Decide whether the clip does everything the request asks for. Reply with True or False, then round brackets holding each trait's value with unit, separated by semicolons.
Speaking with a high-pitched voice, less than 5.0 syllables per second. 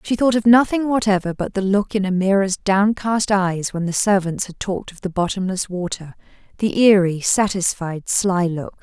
True (195 Hz; 4.8 syllables/s)